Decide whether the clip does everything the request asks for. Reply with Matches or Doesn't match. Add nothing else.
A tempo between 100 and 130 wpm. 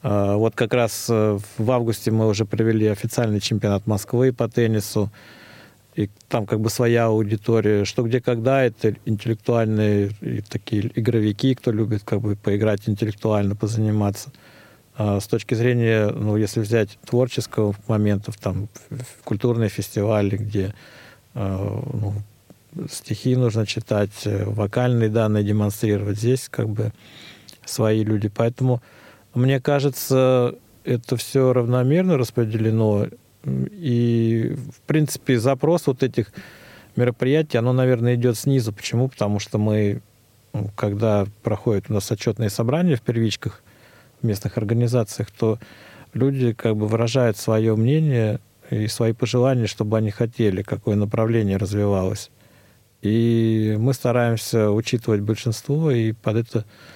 Matches